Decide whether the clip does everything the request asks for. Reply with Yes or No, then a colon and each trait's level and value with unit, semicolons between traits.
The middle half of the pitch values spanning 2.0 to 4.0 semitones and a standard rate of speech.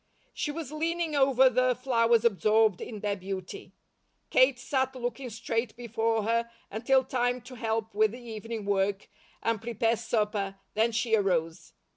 Yes: average, 2.8 semitones; average, 150 wpm